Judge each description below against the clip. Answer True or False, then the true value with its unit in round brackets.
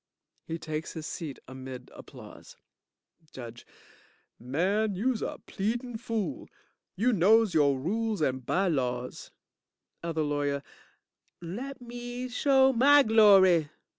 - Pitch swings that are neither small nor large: False (7.8 semitones)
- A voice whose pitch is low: False (190 Hz)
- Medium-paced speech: False (110 wpm)